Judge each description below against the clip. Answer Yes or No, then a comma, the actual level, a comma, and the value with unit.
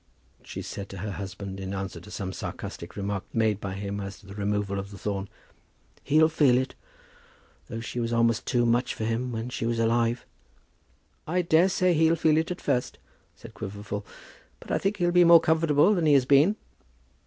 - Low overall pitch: Yes, low, 115 Hz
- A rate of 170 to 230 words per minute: Yes, average, 195 wpm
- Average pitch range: No, wide, 7.5 semitones